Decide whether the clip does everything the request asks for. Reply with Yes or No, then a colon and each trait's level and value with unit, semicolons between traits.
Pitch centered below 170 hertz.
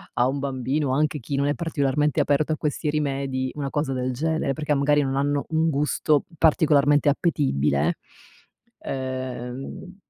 Yes: medium, 140 Hz